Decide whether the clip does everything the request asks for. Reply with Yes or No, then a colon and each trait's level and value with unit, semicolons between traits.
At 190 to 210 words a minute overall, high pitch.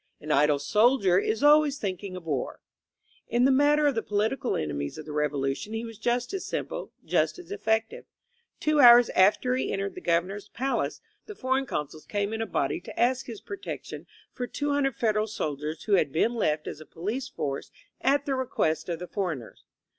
Yes: average, 195 wpm; high, 220 Hz